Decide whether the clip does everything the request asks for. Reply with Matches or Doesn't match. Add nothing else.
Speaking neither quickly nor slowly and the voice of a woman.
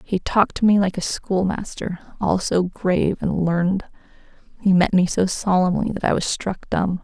Matches